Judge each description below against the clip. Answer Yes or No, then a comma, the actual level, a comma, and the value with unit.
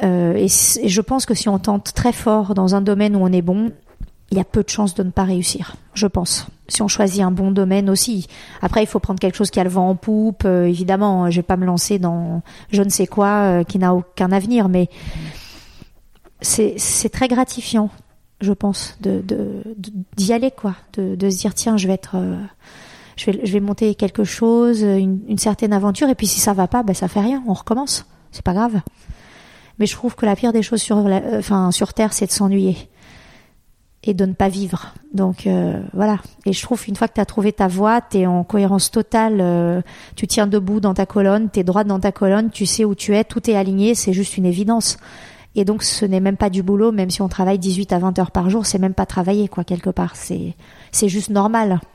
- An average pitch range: No, narrow, 2.1 semitones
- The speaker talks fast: Yes, fast, 240 wpm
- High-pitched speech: Yes, high, 200 Hz